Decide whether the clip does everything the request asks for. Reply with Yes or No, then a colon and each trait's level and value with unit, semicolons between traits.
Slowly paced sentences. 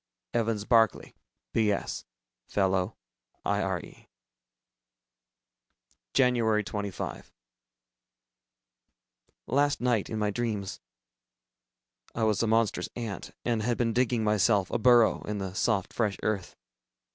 Yes: slow, 100 wpm